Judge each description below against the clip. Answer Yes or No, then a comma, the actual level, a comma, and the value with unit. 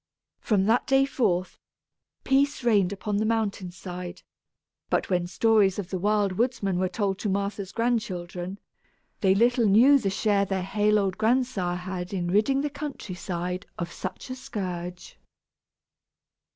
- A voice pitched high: Yes, high, 200 Hz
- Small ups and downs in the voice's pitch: No, average, 3.7 semitones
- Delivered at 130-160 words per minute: Yes, average, 150 wpm